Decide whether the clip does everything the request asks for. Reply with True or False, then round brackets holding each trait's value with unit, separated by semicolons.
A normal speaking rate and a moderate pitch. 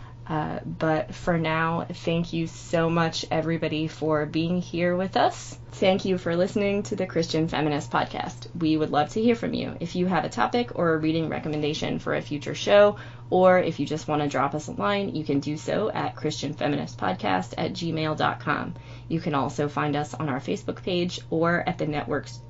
True (195 wpm; 155 Hz)